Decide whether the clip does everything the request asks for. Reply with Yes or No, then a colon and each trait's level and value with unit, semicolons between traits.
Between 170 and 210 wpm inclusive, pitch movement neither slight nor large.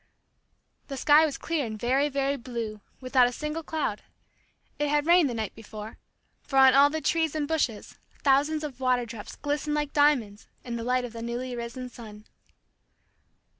Yes: average, 175 wpm; average, 4.0 semitones